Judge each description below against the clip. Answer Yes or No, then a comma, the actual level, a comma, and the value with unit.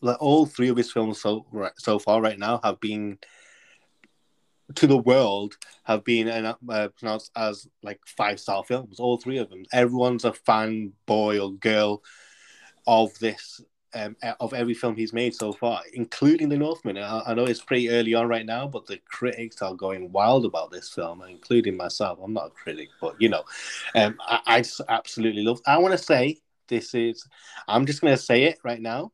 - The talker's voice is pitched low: Yes, low, 115 Hz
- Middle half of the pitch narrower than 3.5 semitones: Yes, narrow, 2.5 semitones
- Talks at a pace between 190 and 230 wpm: Yes, average, 200 wpm